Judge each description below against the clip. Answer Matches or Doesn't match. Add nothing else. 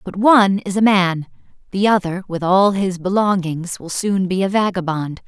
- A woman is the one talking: Matches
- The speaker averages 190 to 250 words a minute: Doesn't match